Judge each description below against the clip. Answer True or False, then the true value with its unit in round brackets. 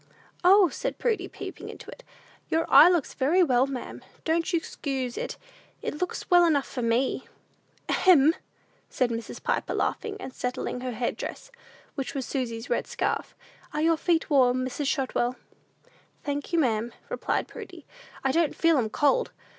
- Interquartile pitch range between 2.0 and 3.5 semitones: False (5.0 semitones)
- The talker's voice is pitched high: True (280 Hz)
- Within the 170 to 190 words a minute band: False (160 wpm)